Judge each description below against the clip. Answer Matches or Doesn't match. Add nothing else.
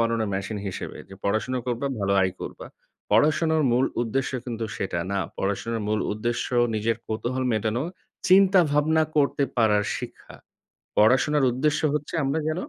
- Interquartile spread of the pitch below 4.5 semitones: Doesn't match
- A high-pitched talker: Doesn't match